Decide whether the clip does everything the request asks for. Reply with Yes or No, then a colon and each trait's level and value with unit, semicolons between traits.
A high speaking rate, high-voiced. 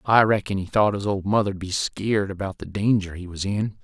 No: fast, 235 wpm; low, 100 Hz